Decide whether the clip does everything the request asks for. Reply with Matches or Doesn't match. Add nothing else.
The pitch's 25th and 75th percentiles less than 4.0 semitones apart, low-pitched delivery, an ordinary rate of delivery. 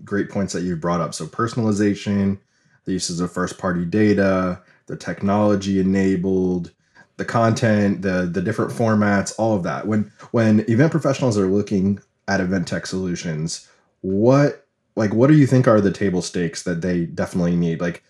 Matches